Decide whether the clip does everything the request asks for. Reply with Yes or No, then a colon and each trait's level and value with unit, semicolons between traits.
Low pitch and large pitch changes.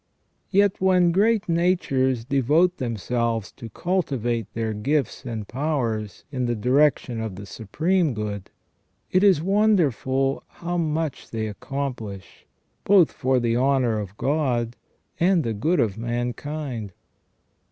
Yes: low, 130 Hz; wide, 6.4 semitones